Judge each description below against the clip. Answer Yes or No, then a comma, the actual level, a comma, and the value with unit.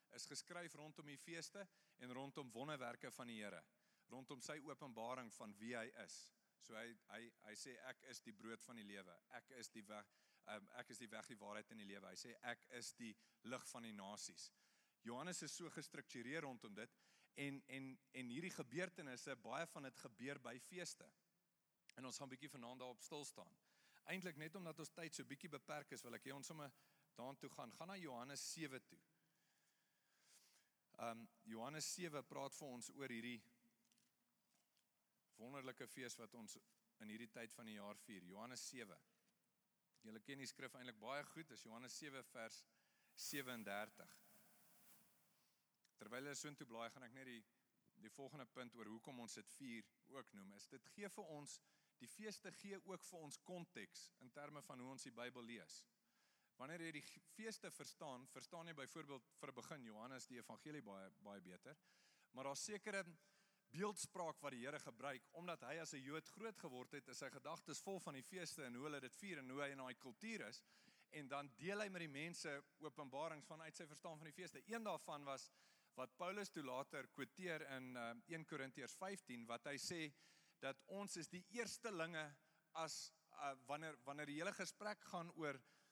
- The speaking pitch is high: No, medium, 140 Hz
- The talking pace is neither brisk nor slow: Yes, average, 185 wpm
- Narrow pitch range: No, average, 5.2 semitones